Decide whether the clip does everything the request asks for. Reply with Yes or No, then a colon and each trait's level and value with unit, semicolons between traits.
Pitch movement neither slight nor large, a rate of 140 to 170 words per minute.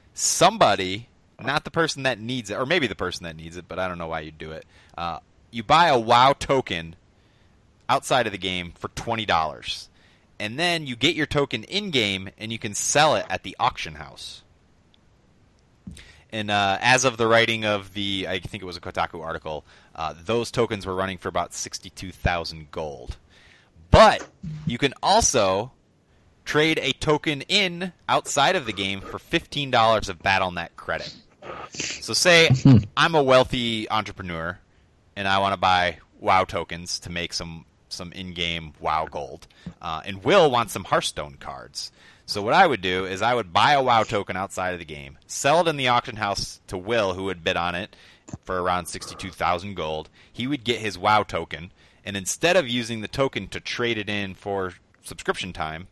No: average, 4.9 semitones; average, 185 wpm